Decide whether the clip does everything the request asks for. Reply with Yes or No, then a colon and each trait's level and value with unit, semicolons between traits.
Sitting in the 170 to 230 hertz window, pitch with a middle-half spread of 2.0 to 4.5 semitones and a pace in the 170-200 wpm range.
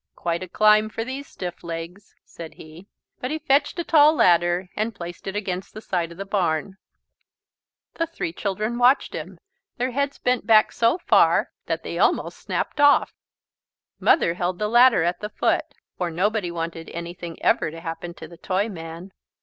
No: high, 190 Hz; average, 5.2 semitones; average, 175 wpm